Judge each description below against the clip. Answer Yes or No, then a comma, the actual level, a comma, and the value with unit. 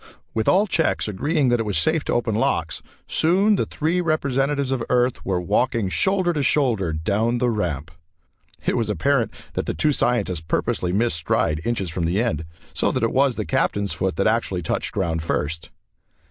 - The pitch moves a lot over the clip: Yes, wide, 7.4 semitones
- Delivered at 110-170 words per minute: No, average, 190 wpm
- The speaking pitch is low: Yes, low, 115 Hz